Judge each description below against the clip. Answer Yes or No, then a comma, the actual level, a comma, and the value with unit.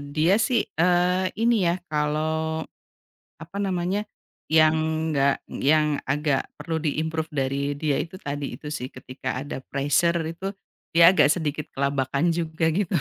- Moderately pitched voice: Yes, medium, 155 Hz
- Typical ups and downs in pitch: Yes, average, 3.0 semitones